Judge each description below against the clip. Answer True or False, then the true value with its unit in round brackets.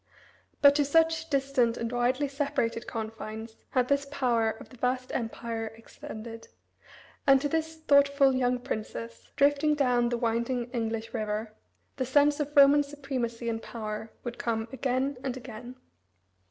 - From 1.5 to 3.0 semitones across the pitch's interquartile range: False (3.6 semitones)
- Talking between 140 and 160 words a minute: True (145 wpm)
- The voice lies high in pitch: True (250 Hz)